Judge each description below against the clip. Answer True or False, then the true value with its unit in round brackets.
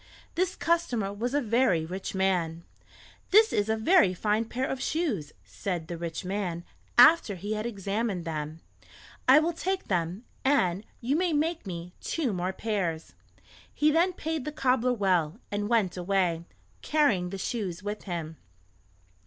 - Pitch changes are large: True (6.9 semitones)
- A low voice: False (205 Hz)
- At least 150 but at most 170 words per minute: True (155 wpm)